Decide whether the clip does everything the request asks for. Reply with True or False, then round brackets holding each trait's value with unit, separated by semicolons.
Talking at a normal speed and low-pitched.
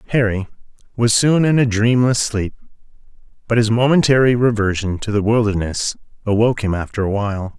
True (150 wpm; 110 Hz)